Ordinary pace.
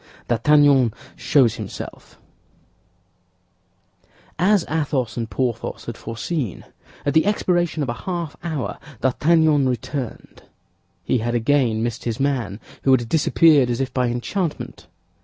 No: slow, 120 wpm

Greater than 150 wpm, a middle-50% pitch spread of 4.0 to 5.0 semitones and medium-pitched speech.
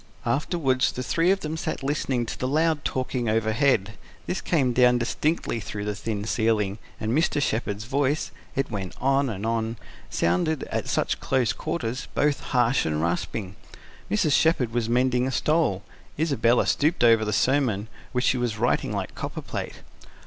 No: average, 165 wpm; average, 4.4 semitones; low, 125 Hz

